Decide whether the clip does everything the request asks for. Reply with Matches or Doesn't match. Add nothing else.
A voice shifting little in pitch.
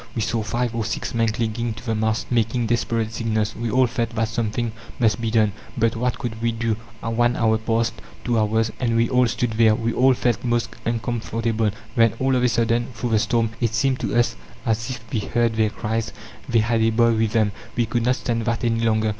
Matches